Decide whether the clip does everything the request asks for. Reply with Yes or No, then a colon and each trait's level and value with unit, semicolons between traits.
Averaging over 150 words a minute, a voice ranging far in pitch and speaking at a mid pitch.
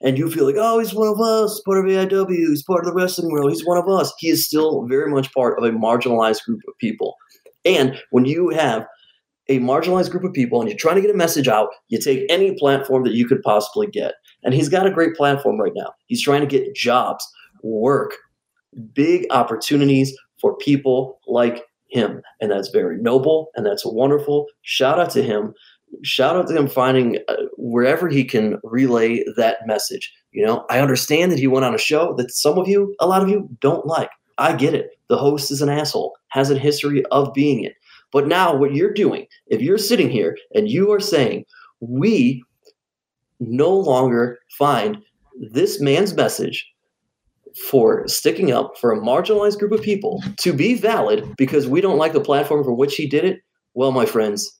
Yes: average, 200 wpm; wide, 7.8 semitones; medium, 150 Hz